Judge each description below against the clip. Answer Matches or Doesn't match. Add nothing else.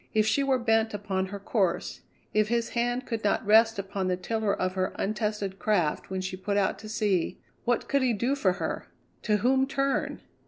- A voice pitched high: Matches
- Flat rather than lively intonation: Doesn't match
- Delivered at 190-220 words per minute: Matches